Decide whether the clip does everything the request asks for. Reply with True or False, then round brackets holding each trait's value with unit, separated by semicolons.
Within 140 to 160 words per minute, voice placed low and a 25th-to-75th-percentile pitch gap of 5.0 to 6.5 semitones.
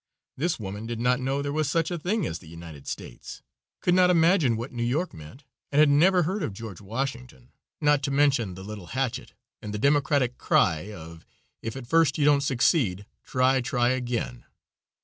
False (190 wpm; 130 Hz; 5.6 semitones)